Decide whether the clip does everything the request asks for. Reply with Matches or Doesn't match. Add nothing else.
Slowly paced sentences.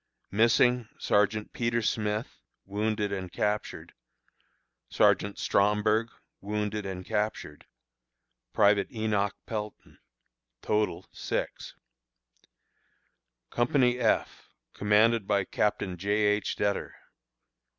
Matches